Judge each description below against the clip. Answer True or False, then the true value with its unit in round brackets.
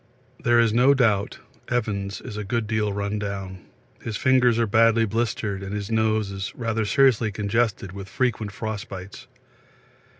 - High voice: False (110 Hz)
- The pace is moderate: True (160 wpm)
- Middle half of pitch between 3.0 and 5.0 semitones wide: False (2.5 semitones)